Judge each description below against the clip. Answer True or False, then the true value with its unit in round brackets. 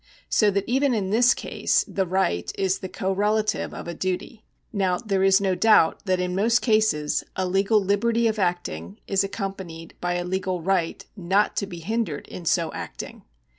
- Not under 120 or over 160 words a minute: False (180 wpm)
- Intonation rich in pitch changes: False (2.9 semitones)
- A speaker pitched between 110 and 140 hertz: False (190 Hz)